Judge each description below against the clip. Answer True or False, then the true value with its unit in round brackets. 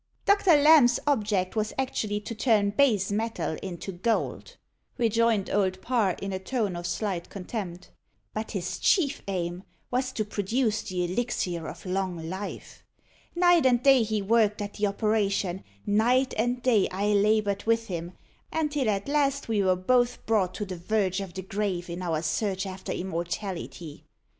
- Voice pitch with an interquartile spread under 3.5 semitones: False (3.9 semitones)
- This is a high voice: True (205 Hz)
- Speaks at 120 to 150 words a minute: False (160 wpm)